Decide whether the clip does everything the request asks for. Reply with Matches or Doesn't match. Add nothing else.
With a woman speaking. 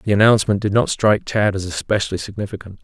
Doesn't match